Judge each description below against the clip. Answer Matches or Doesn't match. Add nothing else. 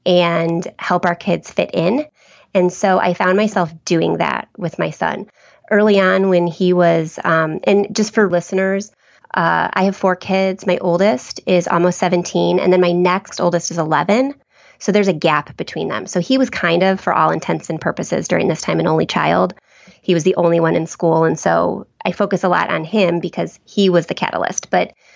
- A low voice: Doesn't match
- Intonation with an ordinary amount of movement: Doesn't match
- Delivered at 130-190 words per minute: Doesn't match